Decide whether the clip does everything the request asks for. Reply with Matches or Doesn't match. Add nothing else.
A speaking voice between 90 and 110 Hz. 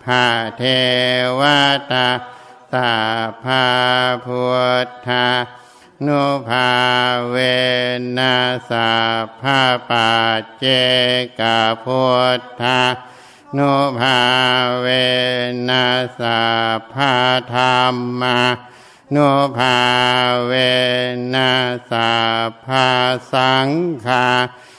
Doesn't match